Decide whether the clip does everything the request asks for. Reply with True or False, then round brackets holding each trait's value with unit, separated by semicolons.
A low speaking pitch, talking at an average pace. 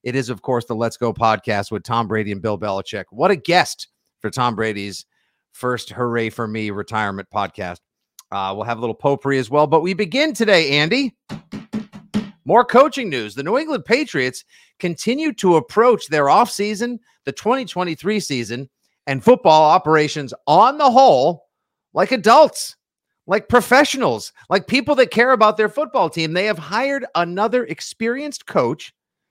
False (170 Hz; 160 wpm)